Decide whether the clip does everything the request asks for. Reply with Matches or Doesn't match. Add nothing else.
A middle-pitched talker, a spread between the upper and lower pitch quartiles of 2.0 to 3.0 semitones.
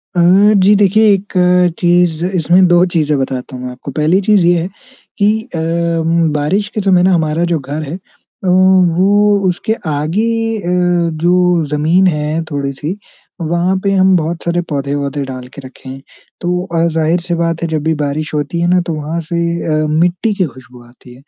Doesn't match